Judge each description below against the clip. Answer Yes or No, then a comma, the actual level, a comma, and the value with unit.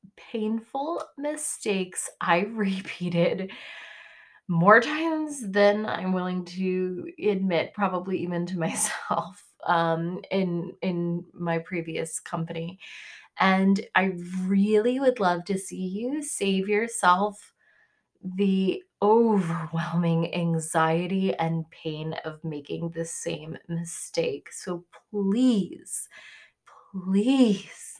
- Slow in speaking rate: Yes, slow, 95 wpm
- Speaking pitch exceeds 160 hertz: Yes, medium, 185 Hz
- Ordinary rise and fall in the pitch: Yes, average, 3.6 semitones